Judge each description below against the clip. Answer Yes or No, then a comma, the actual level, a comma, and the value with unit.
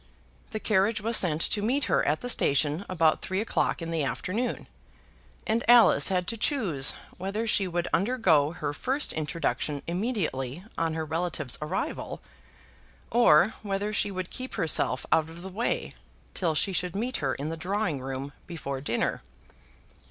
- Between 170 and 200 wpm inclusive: No, average, 160 wpm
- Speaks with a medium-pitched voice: Yes, medium, 180 Hz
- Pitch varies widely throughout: Yes, wide, 5.8 semitones